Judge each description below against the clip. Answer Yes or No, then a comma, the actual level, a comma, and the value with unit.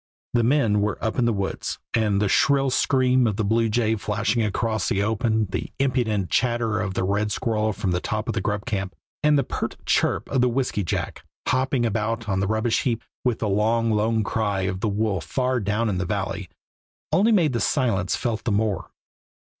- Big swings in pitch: No, average, 2.8 semitones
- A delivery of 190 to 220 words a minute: Yes, average, 200 wpm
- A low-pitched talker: Yes, low, 110 Hz